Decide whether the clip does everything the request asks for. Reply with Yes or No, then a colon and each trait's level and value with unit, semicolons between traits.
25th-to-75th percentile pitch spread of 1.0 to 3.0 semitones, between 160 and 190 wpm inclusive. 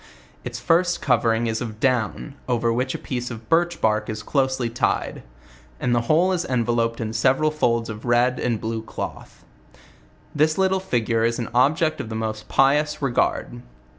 No: average, 4.4 semitones; average, 170 wpm